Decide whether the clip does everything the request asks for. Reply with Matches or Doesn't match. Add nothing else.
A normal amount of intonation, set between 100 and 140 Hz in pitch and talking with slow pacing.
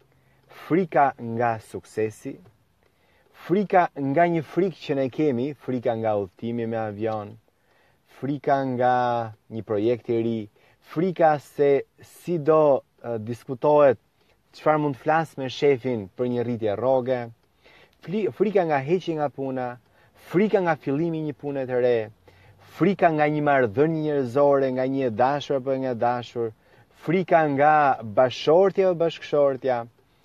Matches